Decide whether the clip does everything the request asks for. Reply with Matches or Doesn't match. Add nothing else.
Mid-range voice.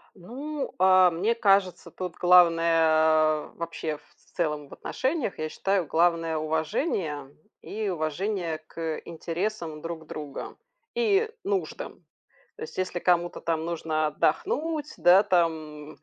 Matches